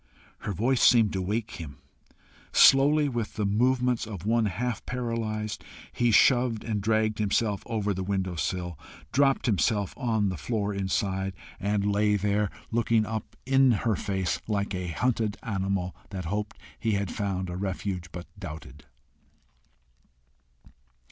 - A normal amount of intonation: Yes, average, 3.2 semitones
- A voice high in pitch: No, low, 105 Hz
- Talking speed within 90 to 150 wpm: Yes, average, 140 wpm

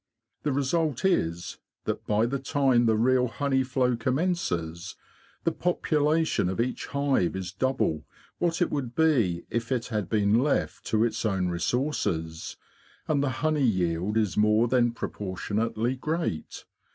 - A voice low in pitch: Yes, low, 120 Hz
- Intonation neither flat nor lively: No, wide, 5.9 semitones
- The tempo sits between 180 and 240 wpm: No, average, 145 wpm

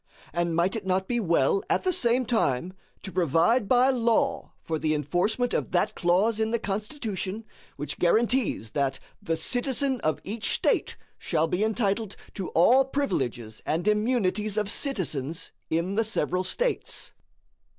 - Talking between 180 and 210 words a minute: No, average, 150 wpm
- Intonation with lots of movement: Yes, wide, 5.7 semitones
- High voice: Yes, high, 200 Hz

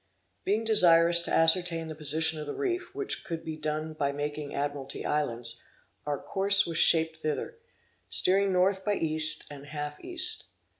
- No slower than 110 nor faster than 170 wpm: Yes, average, 165 wpm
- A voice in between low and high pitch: Yes, medium, 160 Hz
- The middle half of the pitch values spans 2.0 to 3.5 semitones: No, average, 4.0 semitones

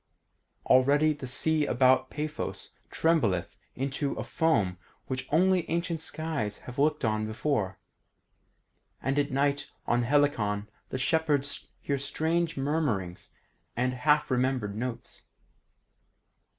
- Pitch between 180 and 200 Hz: No, medium, 140 Hz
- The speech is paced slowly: Yes, slow, 110 wpm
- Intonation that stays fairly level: No, average, 4.0 semitones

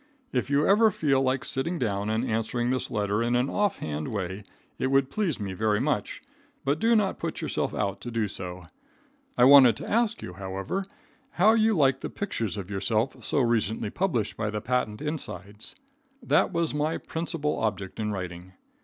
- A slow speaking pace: No, average, 180 wpm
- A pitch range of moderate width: No, wide, 6.5 semitones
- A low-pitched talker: Yes, low, 120 Hz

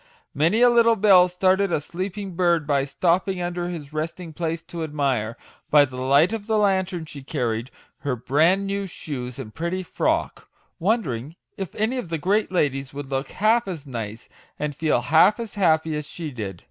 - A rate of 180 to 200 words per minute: Yes, average, 185 wpm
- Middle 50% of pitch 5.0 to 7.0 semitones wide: Yes, average, 5.3 semitones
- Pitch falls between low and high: Yes, medium, 165 Hz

